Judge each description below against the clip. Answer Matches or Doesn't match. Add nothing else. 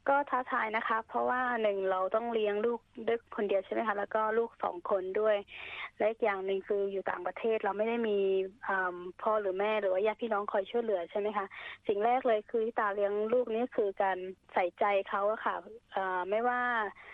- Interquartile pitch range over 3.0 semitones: Doesn't match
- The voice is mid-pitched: Doesn't match